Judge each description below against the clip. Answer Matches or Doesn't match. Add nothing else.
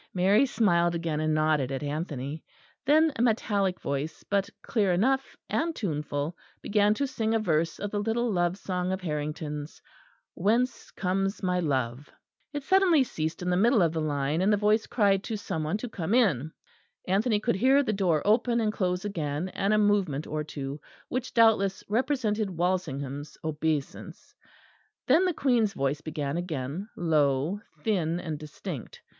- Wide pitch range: Matches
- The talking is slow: Doesn't match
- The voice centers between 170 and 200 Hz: Matches